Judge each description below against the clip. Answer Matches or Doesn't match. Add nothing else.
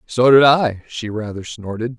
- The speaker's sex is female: Doesn't match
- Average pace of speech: Matches